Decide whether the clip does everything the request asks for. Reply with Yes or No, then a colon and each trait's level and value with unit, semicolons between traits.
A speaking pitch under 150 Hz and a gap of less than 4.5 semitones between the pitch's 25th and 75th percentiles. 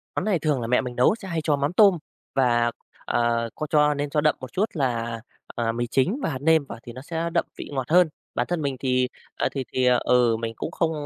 No: low, 135 Hz; average, 4.8 semitones